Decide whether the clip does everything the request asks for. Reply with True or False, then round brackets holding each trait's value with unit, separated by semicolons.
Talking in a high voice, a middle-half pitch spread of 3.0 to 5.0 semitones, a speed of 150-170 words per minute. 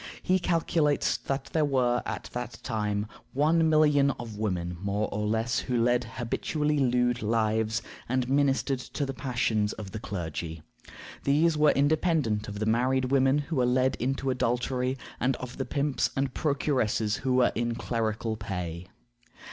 False (125 Hz; 4.0 semitones; 155 wpm)